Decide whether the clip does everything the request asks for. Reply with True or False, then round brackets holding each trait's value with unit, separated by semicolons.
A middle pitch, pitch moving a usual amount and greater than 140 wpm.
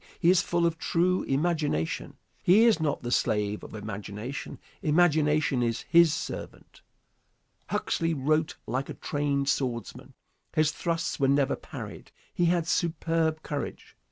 False (155 Hz; 3.8 semitones; 135 wpm)